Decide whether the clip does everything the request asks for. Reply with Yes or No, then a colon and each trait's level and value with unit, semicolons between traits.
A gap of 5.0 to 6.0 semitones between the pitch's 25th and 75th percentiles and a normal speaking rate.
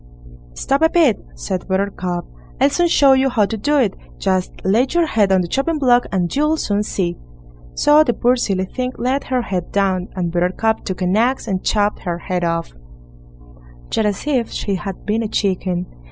Yes: wide, 5.6 semitones; average, 195 wpm